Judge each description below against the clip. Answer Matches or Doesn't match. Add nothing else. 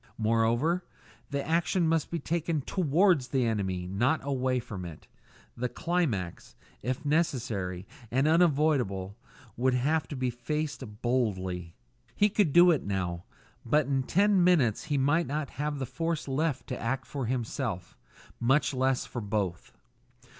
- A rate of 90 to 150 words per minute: Matches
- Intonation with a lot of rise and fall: Matches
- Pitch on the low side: Matches